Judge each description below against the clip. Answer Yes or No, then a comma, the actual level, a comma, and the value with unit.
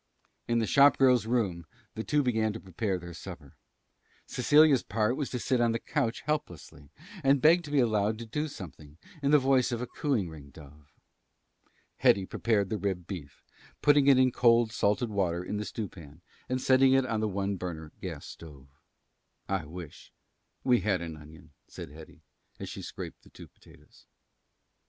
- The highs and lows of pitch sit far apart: Yes, wide, 6.7 semitones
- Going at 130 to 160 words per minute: No, average, 180 wpm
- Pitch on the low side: Yes, low, 110 Hz